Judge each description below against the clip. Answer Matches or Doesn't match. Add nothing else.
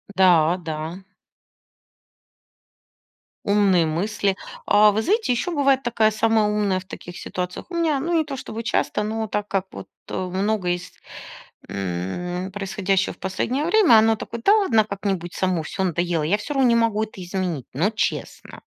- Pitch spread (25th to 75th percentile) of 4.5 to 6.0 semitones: Doesn't match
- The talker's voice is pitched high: Matches